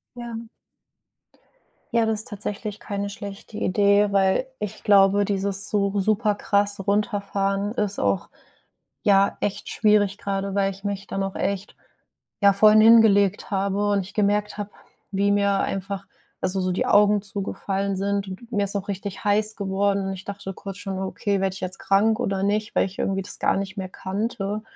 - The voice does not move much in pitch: Yes, narrow, 1.0 semitones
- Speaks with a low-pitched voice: No, high, 200 Hz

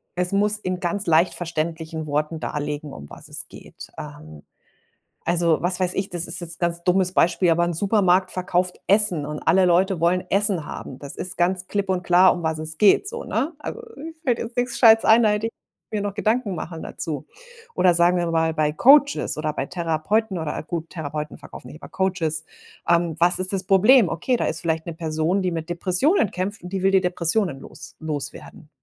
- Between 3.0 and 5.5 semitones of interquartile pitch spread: Yes, average, 3.4 semitones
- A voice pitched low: No, medium, 175 Hz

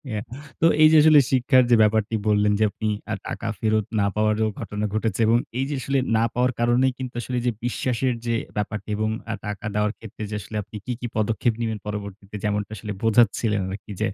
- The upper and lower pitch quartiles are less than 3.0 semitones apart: Yes, narrow, 2.6 semitones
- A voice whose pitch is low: Yes, low, 110 Hz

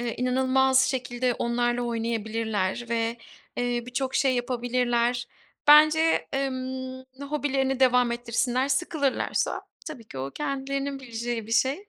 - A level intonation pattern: Yes, narrow, 2.0 semitones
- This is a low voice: No, very high, 250 Hz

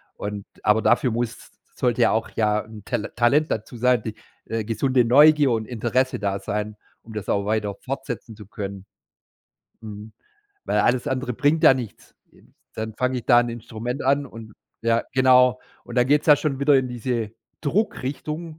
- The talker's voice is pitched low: Yes, low, 120 Hz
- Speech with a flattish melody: No, average, 3.2 semitones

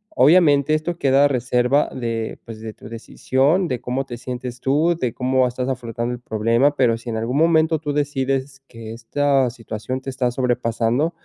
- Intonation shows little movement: No, average, 3.2 semitones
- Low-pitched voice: Yes, low, 130 Hz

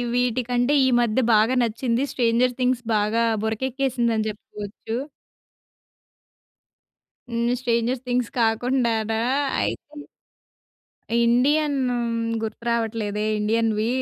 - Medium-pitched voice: No, high, 235 Hz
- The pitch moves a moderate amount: No, narrow, 2.2 semitones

